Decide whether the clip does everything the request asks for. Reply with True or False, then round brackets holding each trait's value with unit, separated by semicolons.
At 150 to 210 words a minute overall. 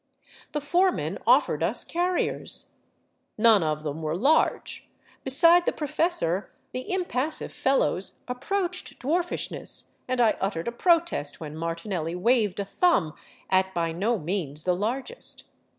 False (135 wpm)